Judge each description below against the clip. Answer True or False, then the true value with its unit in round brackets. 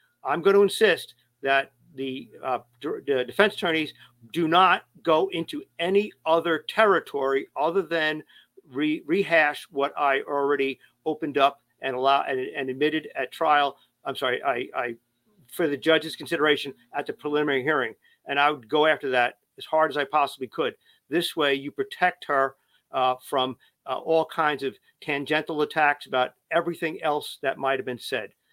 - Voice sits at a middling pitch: True (150 Hz)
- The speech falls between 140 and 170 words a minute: True (165 wpm)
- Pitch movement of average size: True (3.6 semitones)